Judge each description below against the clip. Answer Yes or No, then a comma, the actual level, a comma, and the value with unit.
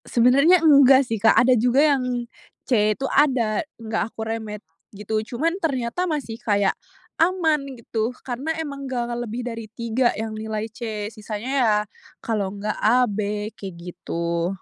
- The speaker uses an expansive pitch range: No, average, 3.7 semitones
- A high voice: Yes, high, 230 Hz